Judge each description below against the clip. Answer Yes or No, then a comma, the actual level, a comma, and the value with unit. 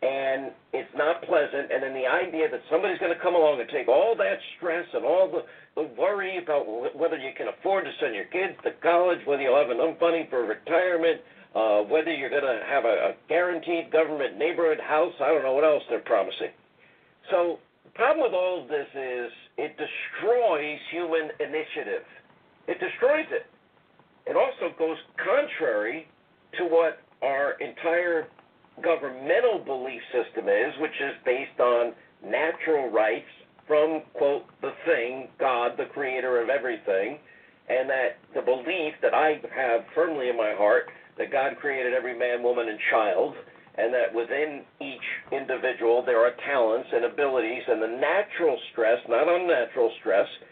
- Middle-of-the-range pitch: Yes, medium, 165 Hz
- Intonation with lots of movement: Yes, wide, 6.6 semitones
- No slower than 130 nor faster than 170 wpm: Yes, average, 165 wpm